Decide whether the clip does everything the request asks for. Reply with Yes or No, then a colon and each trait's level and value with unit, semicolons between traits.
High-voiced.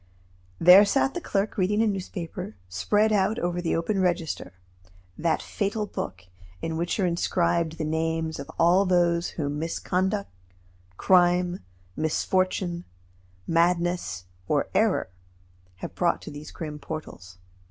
No: medium, 175 Hz